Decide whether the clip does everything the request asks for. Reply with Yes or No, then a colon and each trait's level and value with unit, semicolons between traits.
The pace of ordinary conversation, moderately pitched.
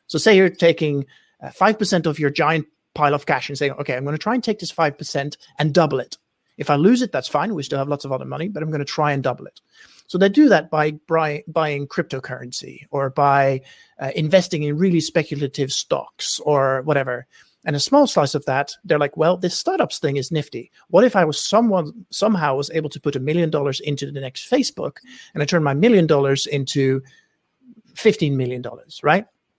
No: fast, 220 wpm; medium, 150 Hz